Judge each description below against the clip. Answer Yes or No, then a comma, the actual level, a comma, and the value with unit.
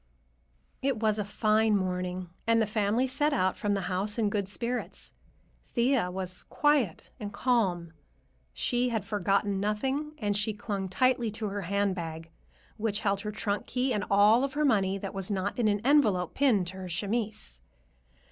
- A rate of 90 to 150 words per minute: No, average, 170 wpm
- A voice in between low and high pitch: No, high, 205 Hz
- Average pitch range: Yes, average, 3.5 semitones